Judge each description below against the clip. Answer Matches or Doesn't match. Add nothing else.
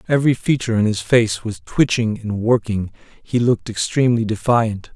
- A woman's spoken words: Doesn't match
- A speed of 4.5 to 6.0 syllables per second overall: Matches